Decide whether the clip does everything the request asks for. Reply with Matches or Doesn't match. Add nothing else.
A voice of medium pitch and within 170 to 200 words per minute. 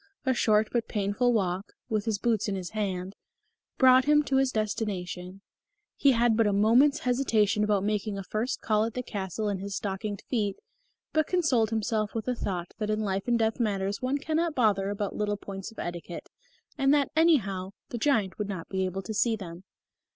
Doesn't match